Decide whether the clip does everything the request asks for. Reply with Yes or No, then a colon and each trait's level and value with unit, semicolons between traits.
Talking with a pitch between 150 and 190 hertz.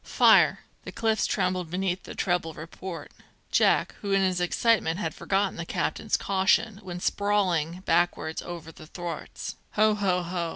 Yes: medium, 185 Hz